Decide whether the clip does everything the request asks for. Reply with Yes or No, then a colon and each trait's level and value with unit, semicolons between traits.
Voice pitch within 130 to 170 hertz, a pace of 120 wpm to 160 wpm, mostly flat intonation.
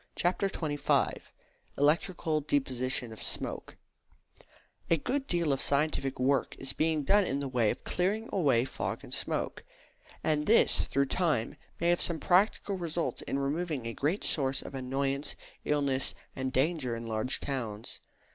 No: medium, 140 Hz; average, 150 wpm; average, 4.4 semitones